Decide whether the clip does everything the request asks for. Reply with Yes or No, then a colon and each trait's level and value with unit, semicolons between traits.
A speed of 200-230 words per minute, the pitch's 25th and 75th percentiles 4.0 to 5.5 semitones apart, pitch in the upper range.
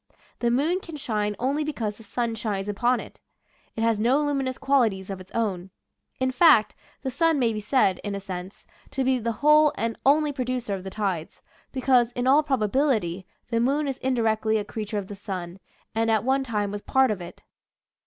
Yes: fast, 205 wpm; average, 4.4 semitones; high, 230 Hz